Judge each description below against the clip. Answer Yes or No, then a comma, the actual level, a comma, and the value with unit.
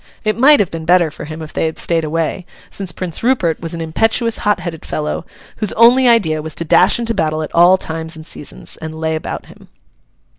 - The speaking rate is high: Yes, fast, 220 wpm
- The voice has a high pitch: No, medium, 165 Hz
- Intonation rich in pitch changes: No, average, 4.8 semitones